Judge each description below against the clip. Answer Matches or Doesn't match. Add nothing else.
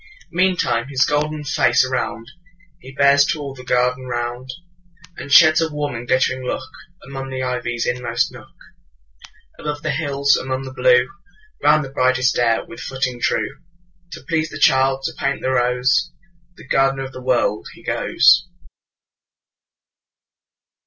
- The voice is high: Doesn't match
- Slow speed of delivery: Matches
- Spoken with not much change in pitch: Doesn't match